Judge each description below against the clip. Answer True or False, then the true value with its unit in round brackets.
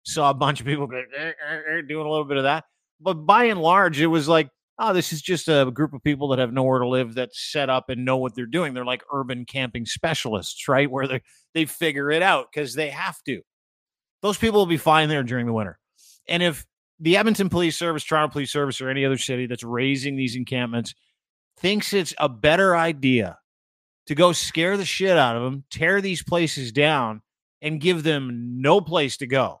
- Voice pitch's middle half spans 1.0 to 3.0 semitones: False (4.2 semitones)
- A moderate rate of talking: False (215 wpm)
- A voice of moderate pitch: True (145 Hz)